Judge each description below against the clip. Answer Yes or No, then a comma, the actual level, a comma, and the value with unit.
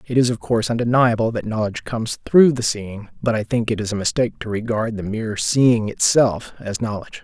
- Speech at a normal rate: No, fast, 215 wpm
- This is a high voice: No, low, 115 Hz